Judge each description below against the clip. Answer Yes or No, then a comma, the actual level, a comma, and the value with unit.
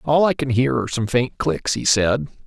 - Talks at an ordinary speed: No, fast, 245 wpm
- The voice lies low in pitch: Yes, low, 120 Hz